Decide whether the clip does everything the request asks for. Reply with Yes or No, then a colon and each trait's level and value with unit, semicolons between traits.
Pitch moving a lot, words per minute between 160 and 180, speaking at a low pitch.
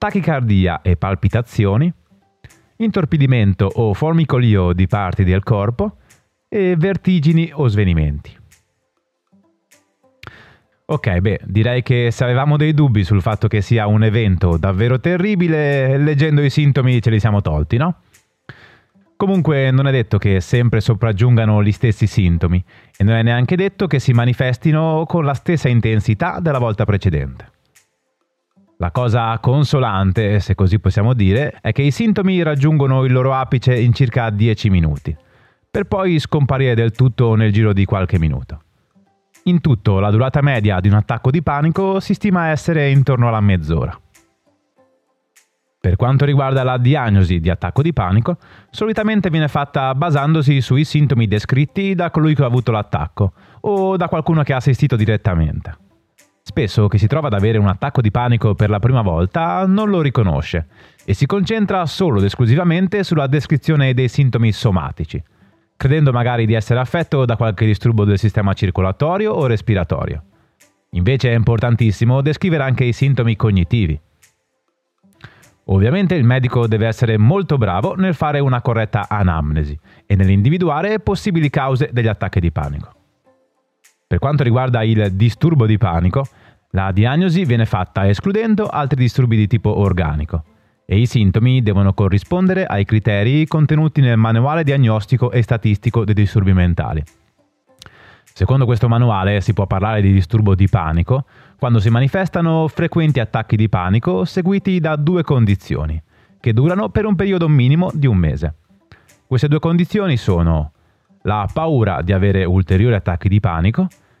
No: wide, 6.5 semitones; average, 150 wpm; low, 120 Hz